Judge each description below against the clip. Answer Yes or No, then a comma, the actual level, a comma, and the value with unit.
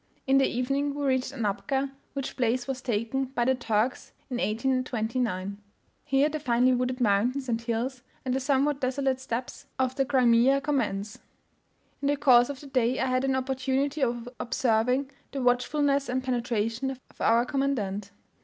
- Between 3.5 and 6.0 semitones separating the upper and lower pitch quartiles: No, narrow, 2.4 semitones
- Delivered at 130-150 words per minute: No, average, 165 wpm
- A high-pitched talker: Yes, very high, 255 Hz